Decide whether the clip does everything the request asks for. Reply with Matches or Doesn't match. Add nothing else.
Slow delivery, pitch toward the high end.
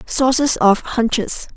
Matches